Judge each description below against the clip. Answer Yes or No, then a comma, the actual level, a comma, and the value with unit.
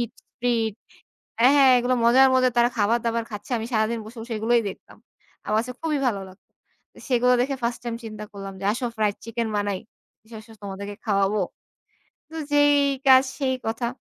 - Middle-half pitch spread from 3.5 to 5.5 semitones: No, average, 2.9 semitones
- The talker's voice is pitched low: No, high, 235 Hz